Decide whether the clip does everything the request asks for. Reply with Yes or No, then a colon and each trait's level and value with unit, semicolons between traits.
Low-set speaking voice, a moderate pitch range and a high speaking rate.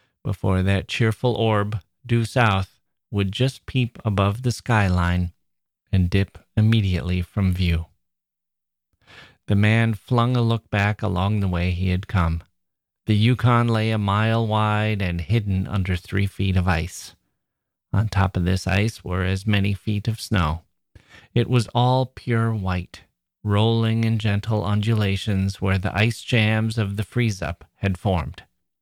No: low, 100 Hz; average, 3.3 semitones; average, 150 wpm